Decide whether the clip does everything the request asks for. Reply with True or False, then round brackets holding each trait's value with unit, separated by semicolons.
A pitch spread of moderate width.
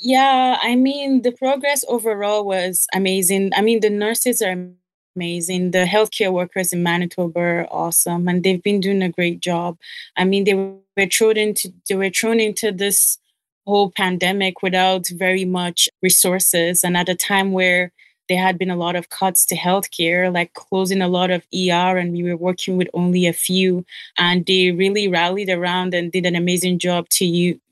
False (1.8 semitones)